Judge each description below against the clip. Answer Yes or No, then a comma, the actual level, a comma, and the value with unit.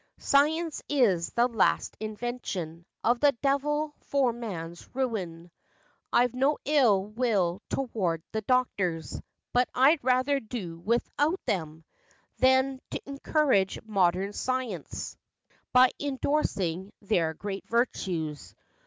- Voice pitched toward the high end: Yes, high, 235 Hz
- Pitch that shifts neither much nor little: No, wide, 6.4 semitones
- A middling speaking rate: No, slow, 110 wpm